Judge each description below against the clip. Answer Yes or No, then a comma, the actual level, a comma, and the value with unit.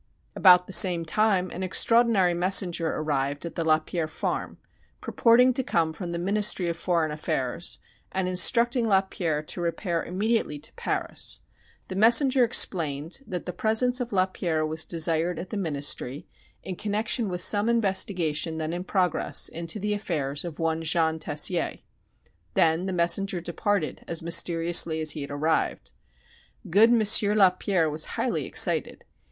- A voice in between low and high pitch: Yes, medium, 175 Hz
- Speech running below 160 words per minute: Yes, average, 150 wpm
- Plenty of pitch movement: No, average, 3.9 semitones